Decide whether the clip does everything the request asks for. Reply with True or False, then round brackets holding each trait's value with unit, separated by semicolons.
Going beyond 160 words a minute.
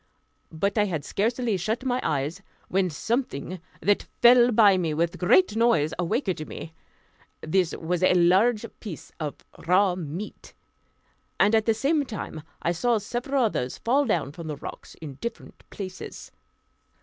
False (155 wpm)